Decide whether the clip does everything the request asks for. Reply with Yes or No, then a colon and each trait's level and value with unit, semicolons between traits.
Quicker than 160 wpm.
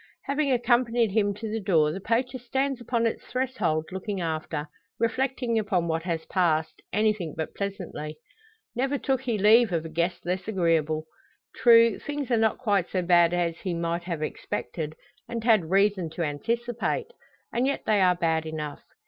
Yes: average, 170 wpm